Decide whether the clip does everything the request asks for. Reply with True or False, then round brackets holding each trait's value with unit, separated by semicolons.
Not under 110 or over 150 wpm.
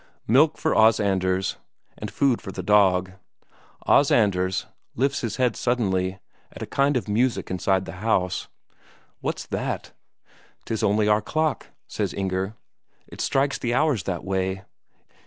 True (145 wpm)